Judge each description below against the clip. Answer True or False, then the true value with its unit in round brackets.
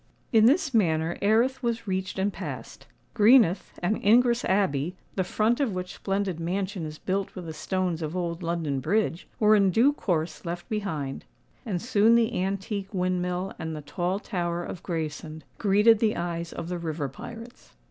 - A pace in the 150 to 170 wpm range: True (165 wpm)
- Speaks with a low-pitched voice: False (185 Hz)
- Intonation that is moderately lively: True (4.2 semitones)